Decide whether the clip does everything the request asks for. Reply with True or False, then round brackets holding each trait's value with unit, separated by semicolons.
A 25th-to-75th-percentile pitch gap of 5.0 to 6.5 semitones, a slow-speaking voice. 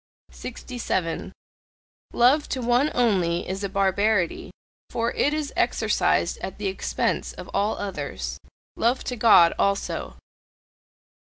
False (4.3 semitones; 115 wpm)